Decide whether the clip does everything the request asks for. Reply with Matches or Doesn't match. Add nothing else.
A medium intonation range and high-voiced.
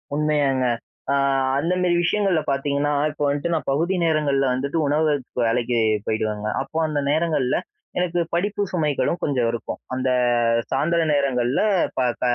Doesn't match